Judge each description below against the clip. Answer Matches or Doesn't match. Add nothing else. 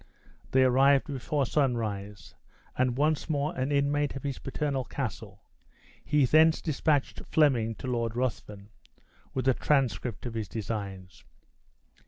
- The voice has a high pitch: Doesn't match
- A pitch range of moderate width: Matches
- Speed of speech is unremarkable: Doesn't match